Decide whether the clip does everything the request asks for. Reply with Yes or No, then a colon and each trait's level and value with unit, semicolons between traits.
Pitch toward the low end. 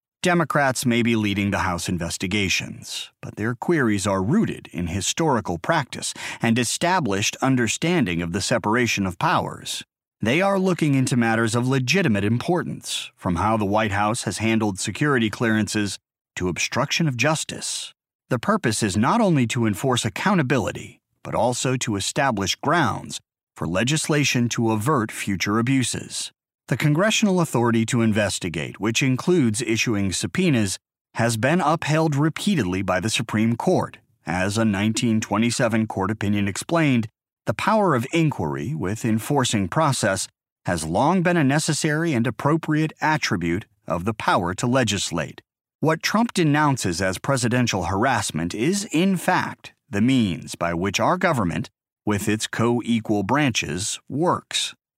Yes: low, 115 Hz